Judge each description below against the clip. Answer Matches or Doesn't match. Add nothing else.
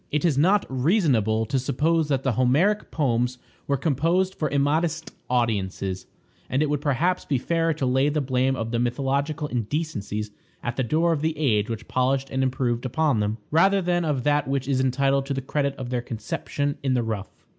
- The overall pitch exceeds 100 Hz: Matches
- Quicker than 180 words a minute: Matches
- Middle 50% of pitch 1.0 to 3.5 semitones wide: Doesn't match